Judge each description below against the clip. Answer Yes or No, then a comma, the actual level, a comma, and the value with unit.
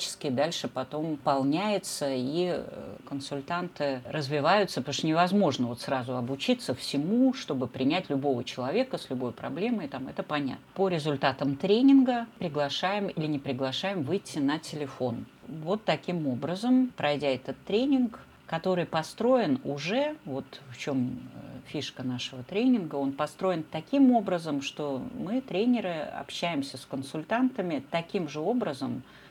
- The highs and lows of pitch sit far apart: Yes, wide, 6.5 semitones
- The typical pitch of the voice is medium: Yes, medium, 155 Hz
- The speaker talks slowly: No, average, 125 wpm